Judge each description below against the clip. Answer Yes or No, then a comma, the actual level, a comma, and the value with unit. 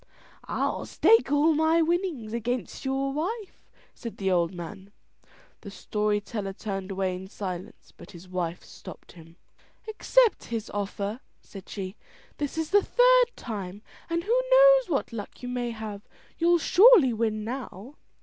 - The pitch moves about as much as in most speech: No, wide, 8.9 semitones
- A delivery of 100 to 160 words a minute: Yes, average, 150 wpm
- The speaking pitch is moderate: No, high, 230 Hz